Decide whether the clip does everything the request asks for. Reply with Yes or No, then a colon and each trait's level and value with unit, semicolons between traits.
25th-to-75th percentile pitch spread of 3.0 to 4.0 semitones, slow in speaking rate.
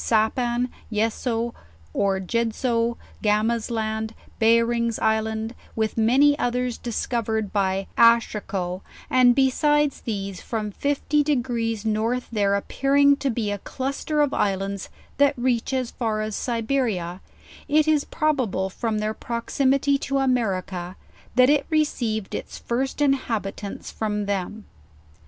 Yes: average, 3.5 semitones; slow, 125 wpm